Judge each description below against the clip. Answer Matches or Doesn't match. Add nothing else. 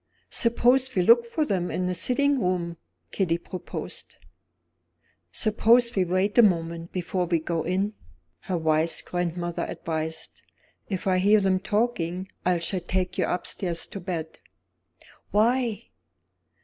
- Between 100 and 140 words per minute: Matches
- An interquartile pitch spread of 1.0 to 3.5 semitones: Doesn't match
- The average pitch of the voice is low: Doesn't match